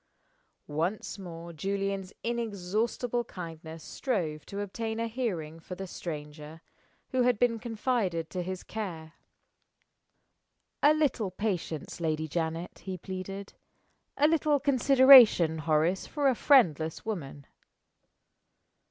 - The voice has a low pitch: No, high, 190 Hz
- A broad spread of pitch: Yes, wide, 6.2 semitones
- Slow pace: Yes, slow, 110 wpm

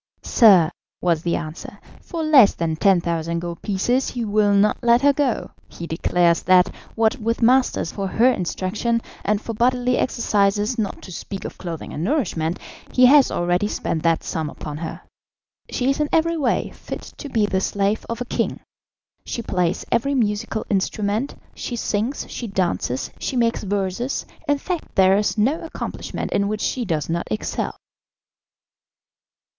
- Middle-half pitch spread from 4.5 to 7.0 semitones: Yes, wide, 5.6 semitones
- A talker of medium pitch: No, high, 210 Hz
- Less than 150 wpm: No, average, 165 wpm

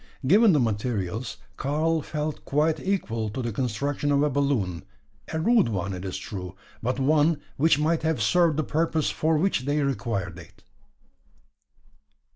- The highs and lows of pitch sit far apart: Yes, wide, 6.2 semitones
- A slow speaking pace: No, average, 155 wpm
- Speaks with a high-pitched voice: No, medium, 140 Hz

